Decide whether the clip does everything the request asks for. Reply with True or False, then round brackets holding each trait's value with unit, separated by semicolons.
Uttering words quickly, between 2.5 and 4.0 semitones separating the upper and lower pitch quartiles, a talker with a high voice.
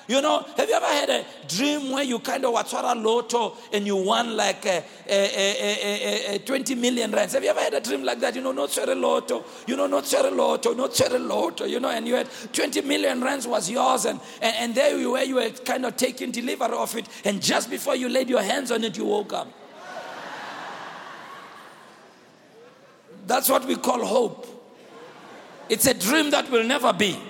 True (215 wpm; 3.7 semitones; 245 Hz)